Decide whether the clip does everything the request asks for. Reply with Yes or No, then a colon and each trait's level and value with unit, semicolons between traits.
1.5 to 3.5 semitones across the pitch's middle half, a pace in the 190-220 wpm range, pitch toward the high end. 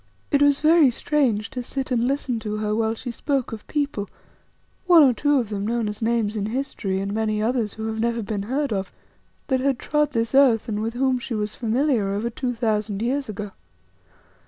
No: average, 4.0 semitones; fast, 205 wpm; high, 230 Hz